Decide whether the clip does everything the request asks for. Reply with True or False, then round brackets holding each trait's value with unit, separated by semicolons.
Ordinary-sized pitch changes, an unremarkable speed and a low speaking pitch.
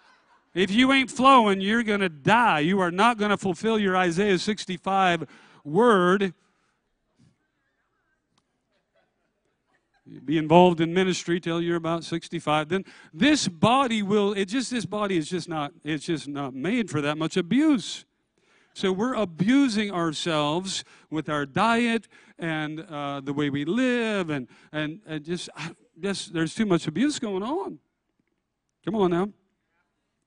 False (5.0 semitones; 145 wpm; 185 Hz)